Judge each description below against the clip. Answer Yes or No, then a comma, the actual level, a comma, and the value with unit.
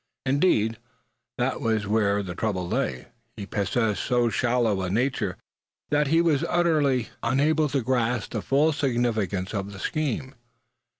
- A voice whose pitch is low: Yes, low, 120 Hz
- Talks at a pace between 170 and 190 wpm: No, average, 140 wpm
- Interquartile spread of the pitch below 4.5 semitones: No, average, 5.2 semitones